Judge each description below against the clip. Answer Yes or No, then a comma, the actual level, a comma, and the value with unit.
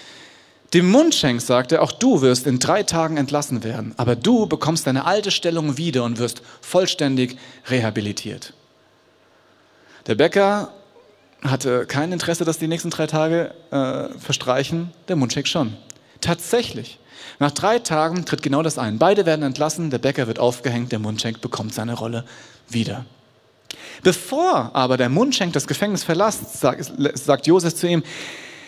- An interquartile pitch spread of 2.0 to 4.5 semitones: No, average, 5.2 semitones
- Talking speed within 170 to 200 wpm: No, average, 145 wpm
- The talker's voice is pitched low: No, medium, 145 Hz